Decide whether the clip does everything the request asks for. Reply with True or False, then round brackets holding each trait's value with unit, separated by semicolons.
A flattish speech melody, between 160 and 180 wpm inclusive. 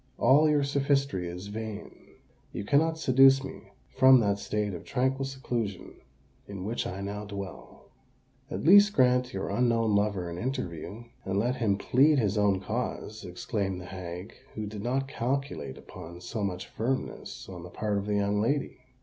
False (5.0 semitones; 165 wpm)